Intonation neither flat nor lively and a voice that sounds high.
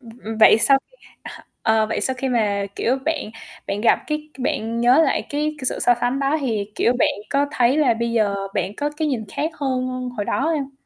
Yes: average, 4.2 semitones; very high, 250 Hz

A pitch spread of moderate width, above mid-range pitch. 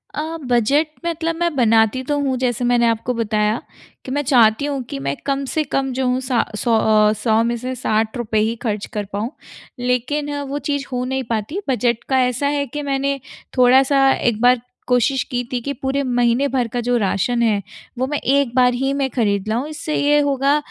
Yes: average, 3.3 semitones; very high, 250 Hz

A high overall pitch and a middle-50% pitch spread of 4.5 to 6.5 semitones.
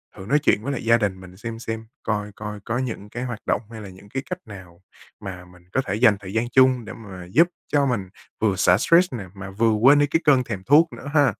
No: low, 110 Hz; average, 4.8 semitones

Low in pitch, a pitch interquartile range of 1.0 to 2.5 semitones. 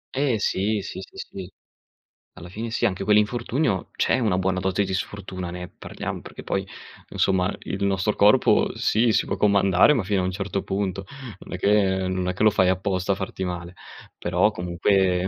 Yes: very low, 95 Hz; narrow, 2.1 semitones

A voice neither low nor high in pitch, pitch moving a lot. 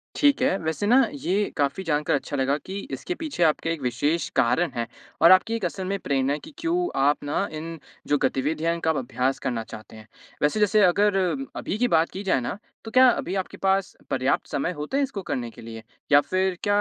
Yes: medium, 165 Hz; wide, 6.2 semitones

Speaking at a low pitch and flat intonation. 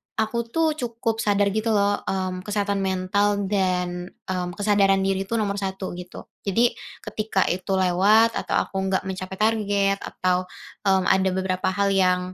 No: high, 195 Hz; narrow, 1.8 semitones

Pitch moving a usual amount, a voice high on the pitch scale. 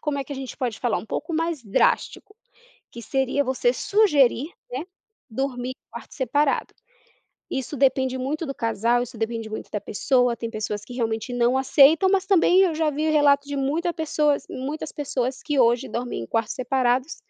Yes: average, 3.7 semitones; very high, 265 Hz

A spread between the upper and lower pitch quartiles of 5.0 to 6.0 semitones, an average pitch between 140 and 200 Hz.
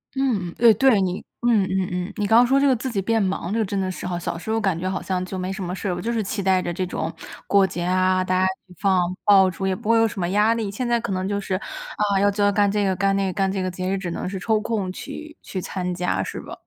No: narrow, 2.6 semitones; high, 195 Hz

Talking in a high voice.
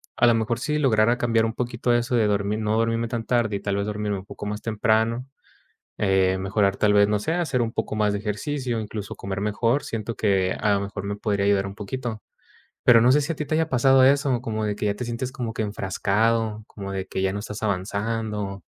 No: low, 110 Hz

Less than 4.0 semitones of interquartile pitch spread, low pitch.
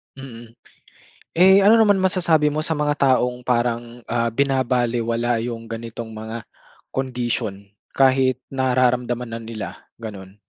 Yes: average, 2.8 semitones; low, 125 Hz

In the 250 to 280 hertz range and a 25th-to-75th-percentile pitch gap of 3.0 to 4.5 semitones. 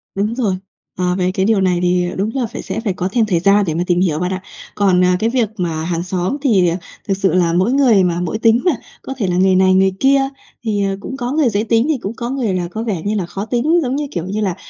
No: high, 195 Hz; average, 4.2 semitones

